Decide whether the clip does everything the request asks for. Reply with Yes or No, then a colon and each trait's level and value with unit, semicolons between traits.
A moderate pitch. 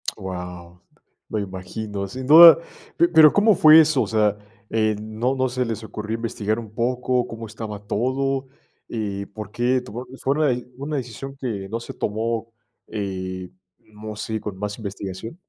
No: low, 110 Hz